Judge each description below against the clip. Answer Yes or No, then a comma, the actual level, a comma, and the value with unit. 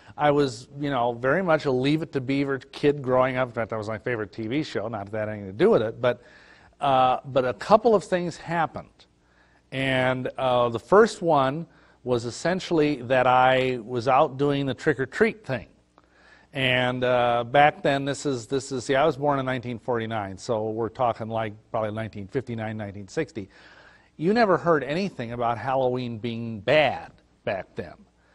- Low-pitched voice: Yes, low, 130 Hz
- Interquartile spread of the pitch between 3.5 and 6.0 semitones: Yes, average, 3.9 semitones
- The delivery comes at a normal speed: Yes, average, 175 wpm